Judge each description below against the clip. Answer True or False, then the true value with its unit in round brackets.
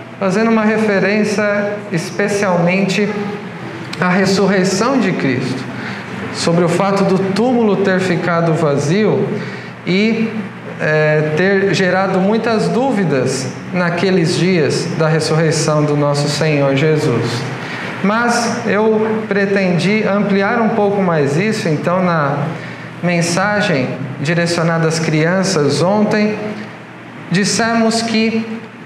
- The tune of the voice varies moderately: True (4.1 semitones)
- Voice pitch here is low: False (190 Hz)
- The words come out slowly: True (100 wpm)